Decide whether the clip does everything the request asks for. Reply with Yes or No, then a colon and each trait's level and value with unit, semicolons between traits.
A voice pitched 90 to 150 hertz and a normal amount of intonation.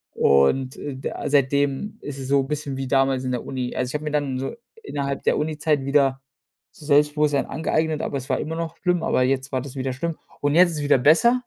No: medium, 140 Hz; narrow, 2.2 semitones